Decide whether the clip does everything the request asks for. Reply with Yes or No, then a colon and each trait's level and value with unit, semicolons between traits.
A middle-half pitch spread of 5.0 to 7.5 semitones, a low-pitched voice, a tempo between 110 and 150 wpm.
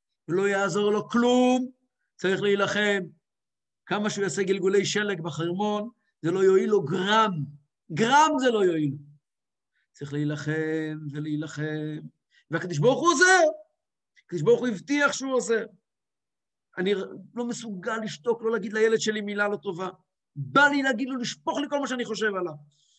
No: wide, 5.6 semitones; high, 200 Hz; average, 145 wpm